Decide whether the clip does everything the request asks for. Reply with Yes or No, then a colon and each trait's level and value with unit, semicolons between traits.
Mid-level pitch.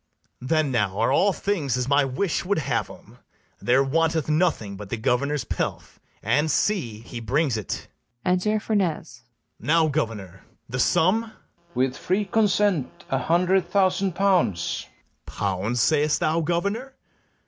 Yes: medium, 155 Hz